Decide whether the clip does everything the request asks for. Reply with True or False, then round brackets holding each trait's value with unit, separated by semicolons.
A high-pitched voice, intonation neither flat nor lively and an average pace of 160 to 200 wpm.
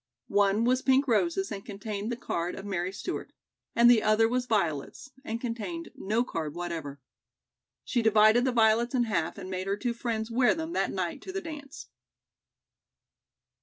True (225 Hz; 4.1 semitones; 170 wpm)